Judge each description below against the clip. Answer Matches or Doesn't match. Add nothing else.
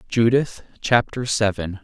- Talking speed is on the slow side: Matches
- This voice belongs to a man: Matches